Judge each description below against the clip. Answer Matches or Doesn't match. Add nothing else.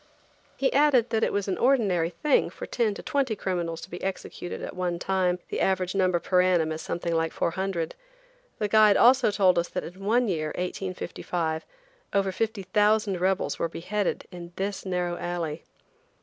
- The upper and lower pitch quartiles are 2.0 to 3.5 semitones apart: Matches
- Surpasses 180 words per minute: Doesn't match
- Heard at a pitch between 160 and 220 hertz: Matches